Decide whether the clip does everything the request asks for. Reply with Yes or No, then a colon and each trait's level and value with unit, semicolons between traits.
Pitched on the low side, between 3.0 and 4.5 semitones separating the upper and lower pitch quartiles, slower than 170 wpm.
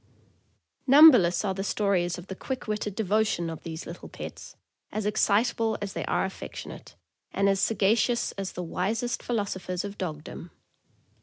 No: high, 200 Hz; average, 3.4 semitones; average, 150 wpm